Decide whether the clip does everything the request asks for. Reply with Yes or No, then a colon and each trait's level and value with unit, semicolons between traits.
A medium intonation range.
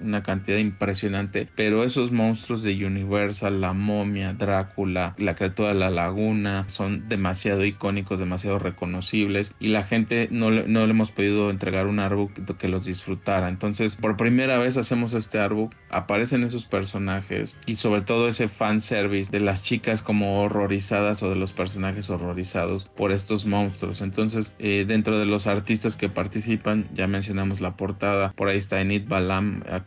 No: narrow, 1.9 semitones